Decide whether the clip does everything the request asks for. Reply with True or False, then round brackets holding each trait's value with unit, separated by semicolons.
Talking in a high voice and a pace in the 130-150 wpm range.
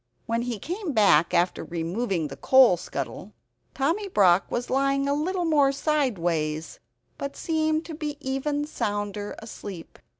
True (250 Hz; 135 wpm)